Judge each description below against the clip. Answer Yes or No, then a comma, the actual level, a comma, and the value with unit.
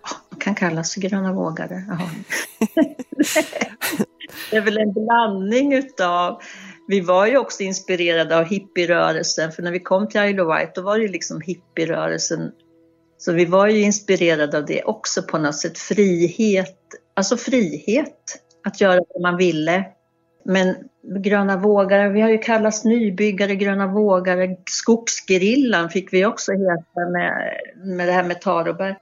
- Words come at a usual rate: Yes, average, 150 wpm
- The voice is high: Yes, high, 195 Hz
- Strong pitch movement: No, average, 3.1 semitones